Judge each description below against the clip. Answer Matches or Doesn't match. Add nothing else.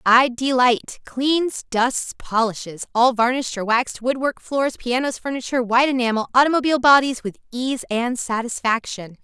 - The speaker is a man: Doesn't match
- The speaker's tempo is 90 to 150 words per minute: Matches